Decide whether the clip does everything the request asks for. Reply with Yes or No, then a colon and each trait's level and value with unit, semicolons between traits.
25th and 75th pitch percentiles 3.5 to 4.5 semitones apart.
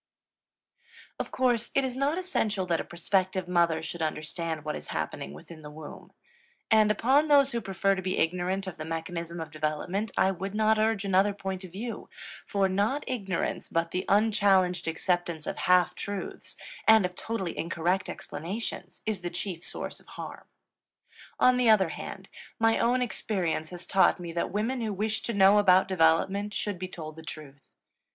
Yes: average, 4.0 semitones